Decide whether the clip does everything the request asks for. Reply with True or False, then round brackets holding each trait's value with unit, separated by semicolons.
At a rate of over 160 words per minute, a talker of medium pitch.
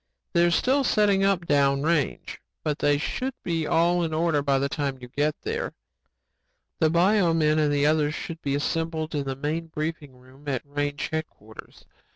True (180 wpm; 155 Hz)